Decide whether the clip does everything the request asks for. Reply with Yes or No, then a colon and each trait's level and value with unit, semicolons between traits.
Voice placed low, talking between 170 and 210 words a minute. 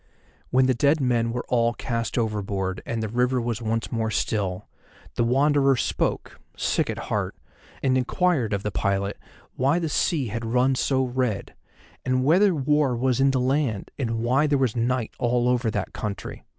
Yes: low, 125 Hz; average, 175 wpm